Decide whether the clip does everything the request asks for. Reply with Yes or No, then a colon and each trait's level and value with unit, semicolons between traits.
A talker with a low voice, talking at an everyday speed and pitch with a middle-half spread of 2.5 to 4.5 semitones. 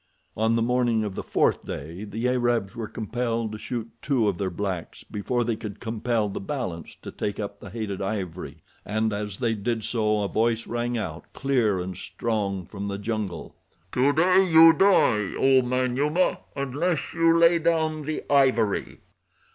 Yes: low, 115 Hz; average, 170 wpm; average, 4.2 semitones